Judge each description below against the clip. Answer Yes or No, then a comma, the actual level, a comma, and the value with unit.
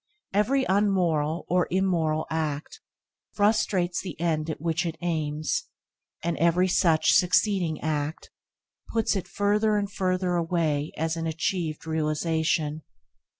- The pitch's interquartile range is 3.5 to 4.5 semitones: No, average, 3.1 semitones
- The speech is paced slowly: Yes, slow, 120 wpm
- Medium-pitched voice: Yes, medium, 170 Hz